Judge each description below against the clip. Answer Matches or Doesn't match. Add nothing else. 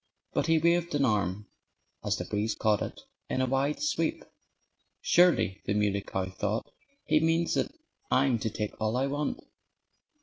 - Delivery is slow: Doesn't match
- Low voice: Matches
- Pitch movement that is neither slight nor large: Doesn't match